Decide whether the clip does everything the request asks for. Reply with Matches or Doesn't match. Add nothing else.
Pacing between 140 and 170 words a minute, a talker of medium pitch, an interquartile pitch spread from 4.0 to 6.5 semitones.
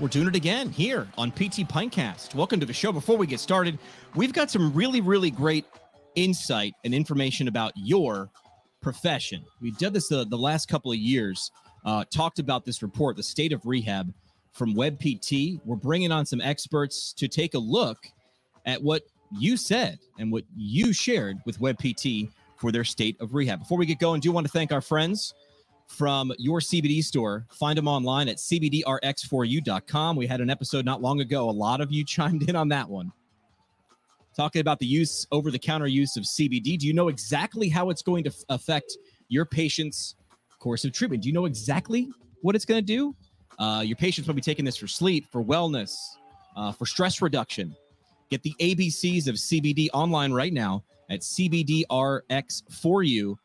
Doesn't match